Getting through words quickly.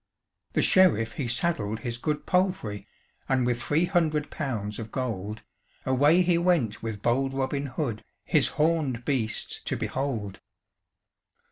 No: slow, 135 wpm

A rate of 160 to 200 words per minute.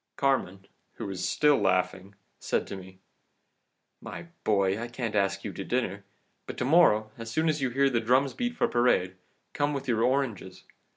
Yes: average, 185 wpm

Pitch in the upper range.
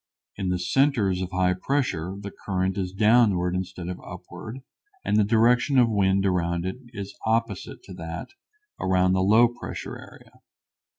No: very low, 95 Hz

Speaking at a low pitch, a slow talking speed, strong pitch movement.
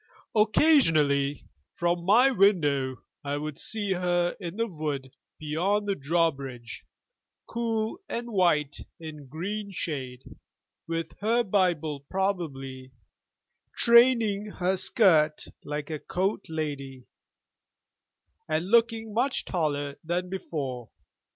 No: medium, 170 Hz; slow, 105 wpm; wide, 6.0 semitones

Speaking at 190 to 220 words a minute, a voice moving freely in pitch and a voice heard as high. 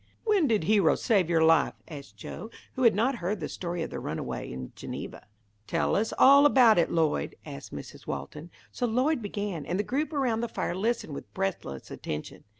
Yes: average, 195 wpm; wide, 6.9 semitones; high, 200 Hz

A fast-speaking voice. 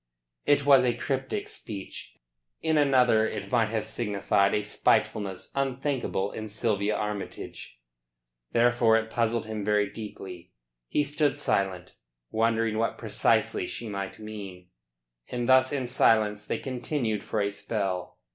No: slow, 135 wpm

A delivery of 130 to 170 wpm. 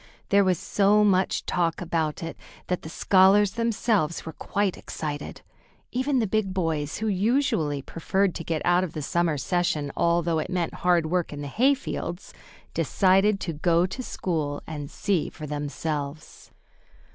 Yes: average, 160 wpm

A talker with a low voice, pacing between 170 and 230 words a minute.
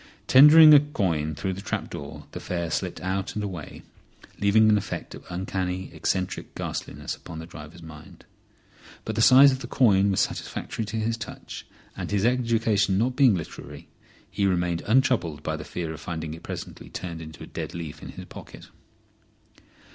Yes: very low, 95 Hz; average, 180 wpm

